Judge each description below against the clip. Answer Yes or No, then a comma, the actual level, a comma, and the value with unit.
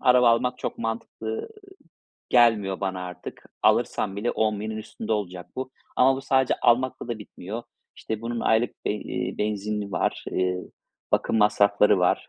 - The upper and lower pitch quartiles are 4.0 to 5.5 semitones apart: No, average, 2.7 semitones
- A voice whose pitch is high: No, low, 110 Hz